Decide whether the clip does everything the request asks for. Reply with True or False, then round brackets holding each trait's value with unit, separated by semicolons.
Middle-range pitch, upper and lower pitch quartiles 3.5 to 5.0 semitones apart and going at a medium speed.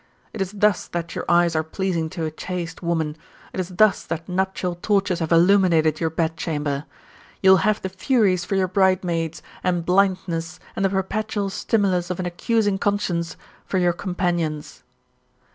False (180 Hz; 2.5 semitones; 165 wpm)